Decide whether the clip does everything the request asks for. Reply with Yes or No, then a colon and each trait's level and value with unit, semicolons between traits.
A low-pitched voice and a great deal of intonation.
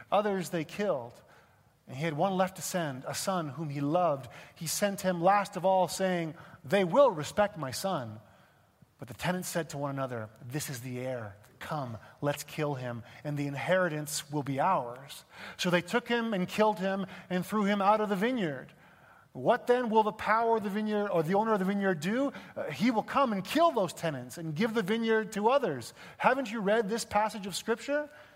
No: medium, 185 Hz; wide, 6.2 semitones